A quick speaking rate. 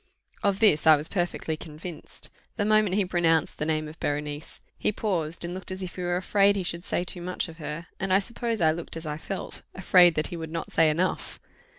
Yes: fast, 230 wpm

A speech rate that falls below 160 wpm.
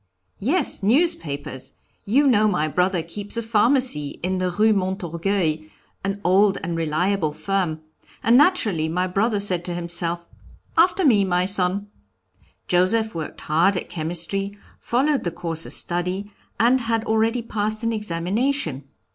Yes: average, 140 wpm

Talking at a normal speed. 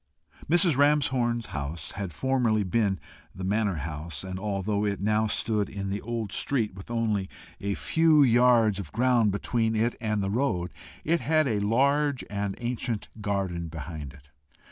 Yes: average, 160 wpm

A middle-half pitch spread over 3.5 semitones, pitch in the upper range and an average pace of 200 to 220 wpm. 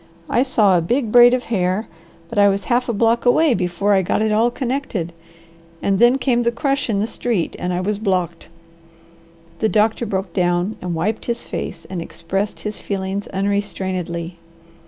No: average, 4.3 semitones; high, 205 Hz; average, 180 wpm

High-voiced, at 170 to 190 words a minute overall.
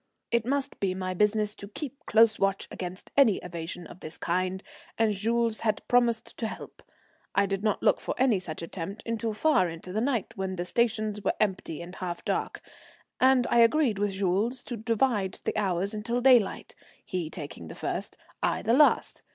Yes: high, 210 Hz; average, 185 wpm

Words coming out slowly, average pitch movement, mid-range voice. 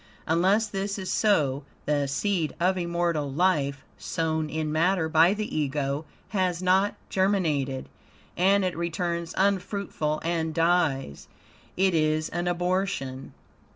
Yes: slow, 120 wpm; average, 3.6 semitones; medium, 170 Hz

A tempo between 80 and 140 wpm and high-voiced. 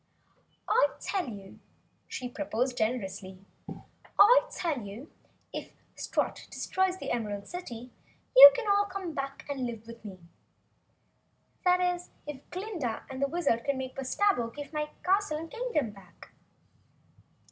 Yes: slow, 135 wpm; very high, 275 Hz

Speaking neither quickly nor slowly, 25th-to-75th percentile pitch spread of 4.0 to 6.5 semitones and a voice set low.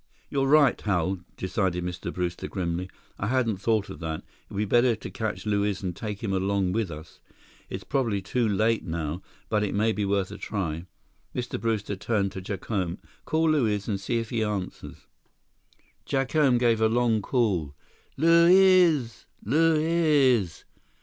Yes: average, 160 wpm; average, 4.5 semitones; low, 105 Hz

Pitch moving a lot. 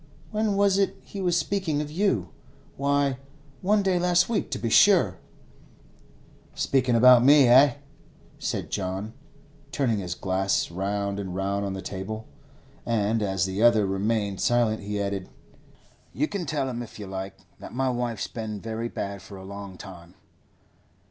Yes: wide, 6.4 semitones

